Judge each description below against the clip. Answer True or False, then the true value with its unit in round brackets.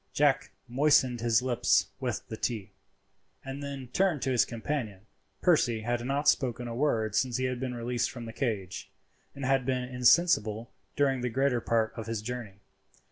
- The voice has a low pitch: True (125 Hz)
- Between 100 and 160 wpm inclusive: False (175 wpm)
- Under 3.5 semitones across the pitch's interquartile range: True (2.7 semitones)